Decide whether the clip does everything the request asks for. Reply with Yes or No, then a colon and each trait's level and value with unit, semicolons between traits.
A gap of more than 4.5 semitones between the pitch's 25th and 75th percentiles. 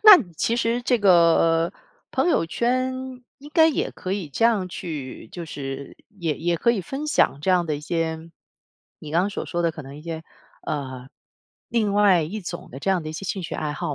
Yes: average, 5.0 semitones